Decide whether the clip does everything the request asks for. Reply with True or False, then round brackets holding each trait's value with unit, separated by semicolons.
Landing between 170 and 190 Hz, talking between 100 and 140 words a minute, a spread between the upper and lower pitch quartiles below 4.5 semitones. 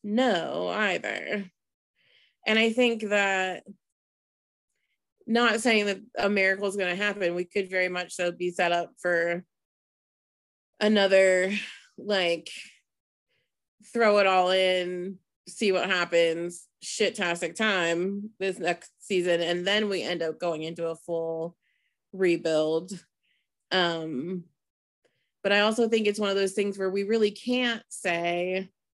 True (185 Hz; 135 wpm; 3.1 semitones)